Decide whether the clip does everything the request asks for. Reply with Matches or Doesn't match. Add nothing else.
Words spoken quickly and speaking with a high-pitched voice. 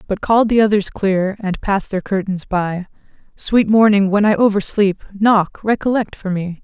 Doesn't match